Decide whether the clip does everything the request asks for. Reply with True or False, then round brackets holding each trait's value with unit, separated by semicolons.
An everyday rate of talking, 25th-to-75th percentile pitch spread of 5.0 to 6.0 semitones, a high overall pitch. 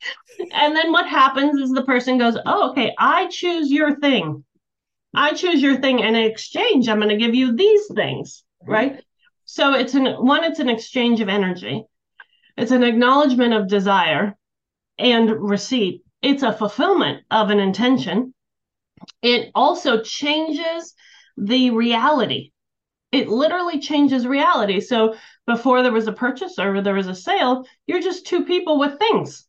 True (155 wpm; 5.6 semitones; 260 Hz)